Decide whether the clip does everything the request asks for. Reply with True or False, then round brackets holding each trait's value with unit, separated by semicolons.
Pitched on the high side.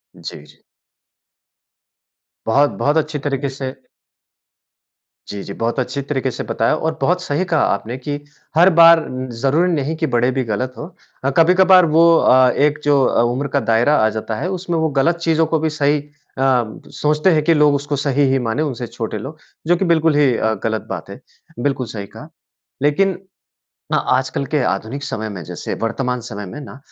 False (145 Hz)